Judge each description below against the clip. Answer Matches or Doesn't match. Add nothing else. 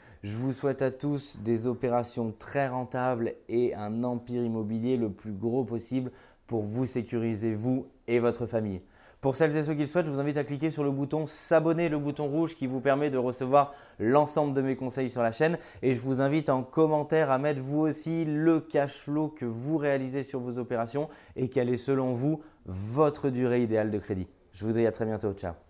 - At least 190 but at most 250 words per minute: Matches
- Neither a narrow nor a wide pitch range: Matches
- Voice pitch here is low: Matches